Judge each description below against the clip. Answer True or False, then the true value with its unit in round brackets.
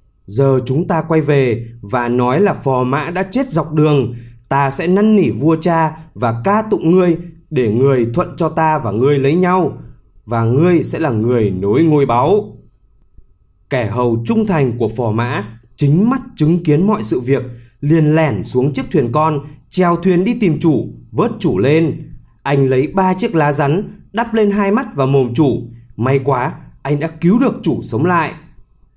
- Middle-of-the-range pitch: True (145 Hz)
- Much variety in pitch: True (5.8 semitones)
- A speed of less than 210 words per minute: True (190 wpm)